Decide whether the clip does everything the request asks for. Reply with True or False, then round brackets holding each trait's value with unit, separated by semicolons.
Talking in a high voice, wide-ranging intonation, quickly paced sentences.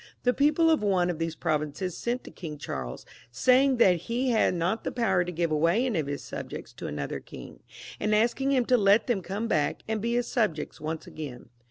True (195 Hz; 7.2 semitones; 215 wpm)